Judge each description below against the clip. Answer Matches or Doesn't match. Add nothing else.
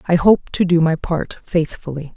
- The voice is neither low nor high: Matches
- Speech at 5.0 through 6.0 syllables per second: Doesn't match